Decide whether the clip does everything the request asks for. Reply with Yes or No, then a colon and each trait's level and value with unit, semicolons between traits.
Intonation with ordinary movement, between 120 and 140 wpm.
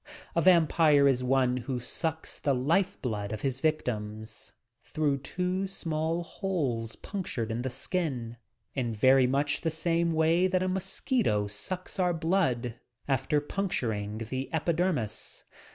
No: wide, 5.9 semitones; slow, 135 wpm